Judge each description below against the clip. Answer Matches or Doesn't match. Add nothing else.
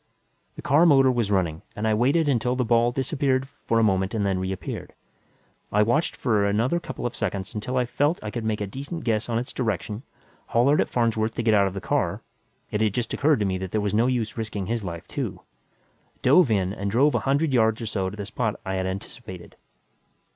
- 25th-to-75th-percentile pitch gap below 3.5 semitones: Doesn't match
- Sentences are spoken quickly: Matches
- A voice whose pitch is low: Matches